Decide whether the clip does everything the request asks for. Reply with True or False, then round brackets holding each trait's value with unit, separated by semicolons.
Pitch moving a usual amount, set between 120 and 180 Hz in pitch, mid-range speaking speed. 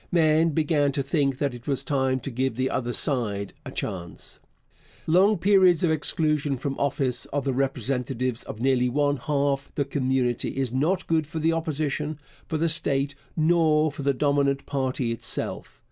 True (3.0 semitones; 140 Hz; 170 wpm)